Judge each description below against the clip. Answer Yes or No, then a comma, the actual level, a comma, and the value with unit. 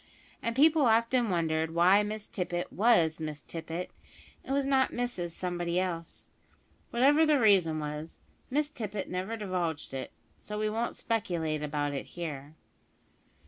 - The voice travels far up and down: Yes, wide, 6.1 semitones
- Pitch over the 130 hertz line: Yes, medium, 185 Hz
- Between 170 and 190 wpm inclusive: No, average, 145 wpm